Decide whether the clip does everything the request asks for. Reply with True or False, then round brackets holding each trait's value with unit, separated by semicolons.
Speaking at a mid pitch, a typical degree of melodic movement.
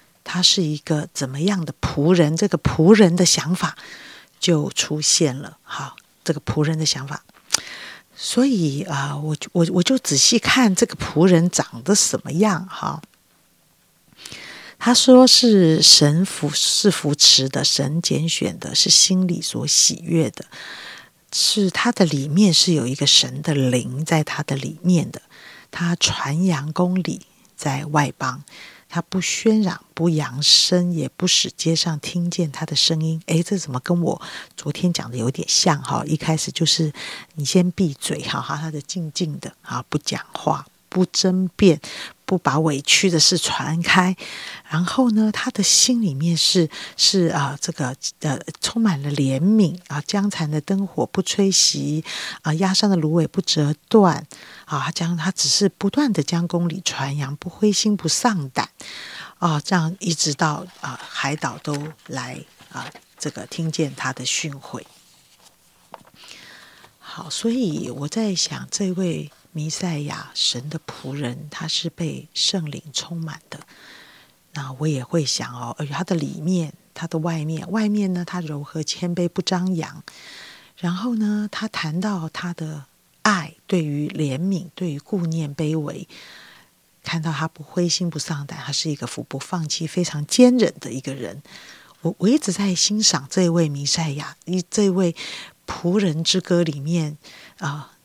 True (165 Hz; 3.7 semitones)